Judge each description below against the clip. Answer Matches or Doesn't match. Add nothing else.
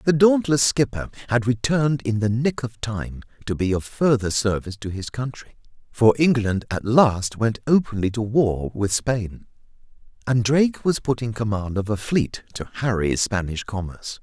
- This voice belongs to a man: Matches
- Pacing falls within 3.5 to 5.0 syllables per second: Matches